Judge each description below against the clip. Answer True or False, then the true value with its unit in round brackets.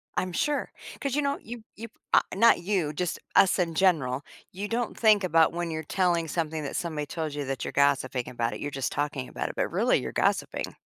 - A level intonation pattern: False (5.1 semitones)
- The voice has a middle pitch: True (165 Hz)